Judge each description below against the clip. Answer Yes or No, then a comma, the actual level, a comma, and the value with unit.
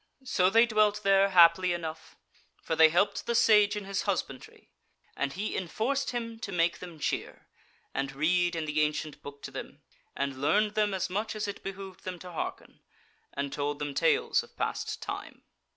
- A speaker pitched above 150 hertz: Yes, medium, 185 Hz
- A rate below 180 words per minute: No, average, 185 wpm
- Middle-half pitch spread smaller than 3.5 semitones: No, average, 5.0 semitones